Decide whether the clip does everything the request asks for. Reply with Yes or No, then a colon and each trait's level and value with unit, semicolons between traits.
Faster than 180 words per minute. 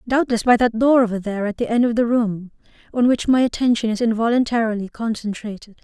Yes: average, 195 wpm